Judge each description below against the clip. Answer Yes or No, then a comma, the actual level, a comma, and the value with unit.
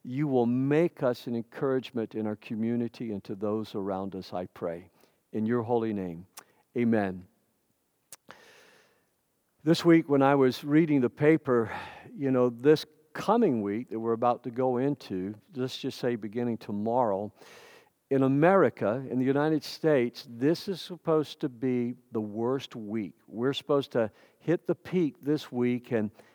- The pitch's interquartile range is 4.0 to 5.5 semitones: Yes, average, 4.3 semitones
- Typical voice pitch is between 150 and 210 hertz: No, low, 125 Hz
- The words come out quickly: No, average, 155 wpm